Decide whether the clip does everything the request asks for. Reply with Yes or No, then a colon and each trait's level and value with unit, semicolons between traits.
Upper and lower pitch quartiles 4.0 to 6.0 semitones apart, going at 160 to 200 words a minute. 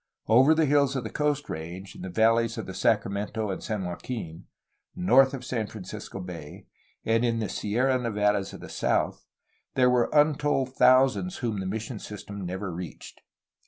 Yes: average, 4.7 semitones; average, 170 wpm